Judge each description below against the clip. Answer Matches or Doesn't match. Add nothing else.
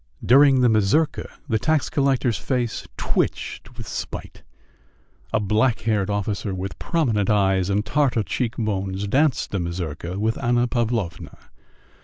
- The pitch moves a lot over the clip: Doesn't match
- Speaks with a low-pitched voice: Matches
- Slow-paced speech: Matches